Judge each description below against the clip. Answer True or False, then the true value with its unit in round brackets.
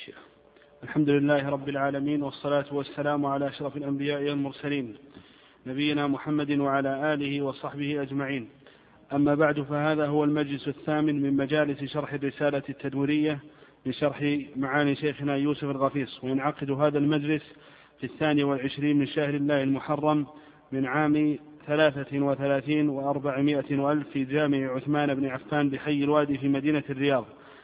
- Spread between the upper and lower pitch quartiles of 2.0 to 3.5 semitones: False (1.1 semitones)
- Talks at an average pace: True (125 wpm)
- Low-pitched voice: False (145 Hz)